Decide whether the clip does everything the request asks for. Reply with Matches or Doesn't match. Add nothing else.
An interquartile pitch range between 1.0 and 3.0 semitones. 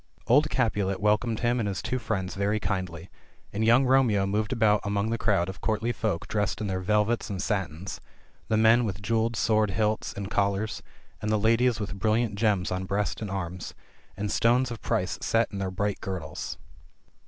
Matches